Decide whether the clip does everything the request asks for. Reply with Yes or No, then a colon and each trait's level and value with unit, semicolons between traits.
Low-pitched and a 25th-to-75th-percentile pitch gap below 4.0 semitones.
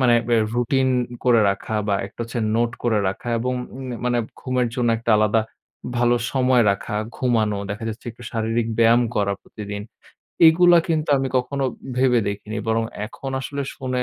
Yes: low, 120 Hz; narrow, 2.5 semitones